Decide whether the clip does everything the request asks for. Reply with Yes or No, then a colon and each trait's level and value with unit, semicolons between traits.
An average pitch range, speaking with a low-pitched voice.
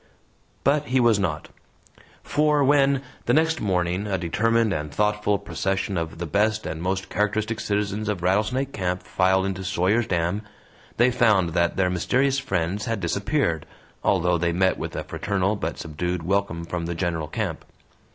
Yes: average, 4.0 semitones; very low, 95 Hz